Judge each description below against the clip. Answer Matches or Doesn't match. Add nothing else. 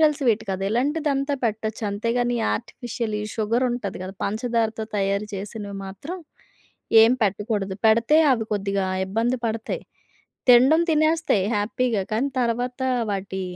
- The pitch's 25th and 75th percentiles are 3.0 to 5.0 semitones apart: Matches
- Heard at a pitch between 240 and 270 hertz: Doesn't match